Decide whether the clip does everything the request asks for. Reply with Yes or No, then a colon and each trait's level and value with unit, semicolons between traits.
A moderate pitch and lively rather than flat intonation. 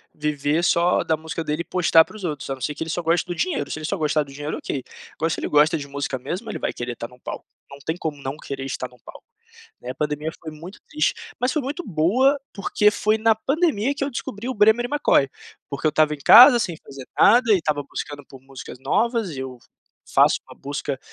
Yes: medium, 160 Hz; wide, 7.3 semitones